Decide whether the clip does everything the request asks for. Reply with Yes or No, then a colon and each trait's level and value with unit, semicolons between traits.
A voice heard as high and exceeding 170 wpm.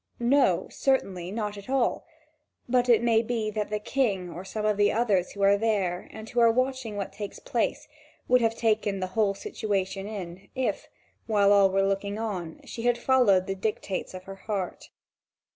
Yes: high, 210 Hz; average, 185 wpm